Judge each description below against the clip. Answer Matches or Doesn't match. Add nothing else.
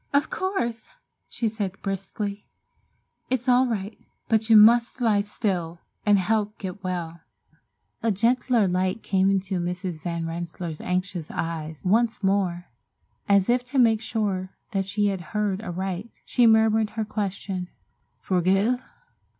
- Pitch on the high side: Matches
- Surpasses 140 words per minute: Doesn't match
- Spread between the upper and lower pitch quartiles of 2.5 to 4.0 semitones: Matches